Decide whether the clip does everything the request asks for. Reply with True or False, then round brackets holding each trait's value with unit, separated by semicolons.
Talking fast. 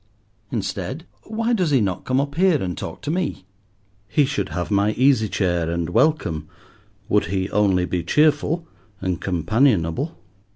False (155 wpm)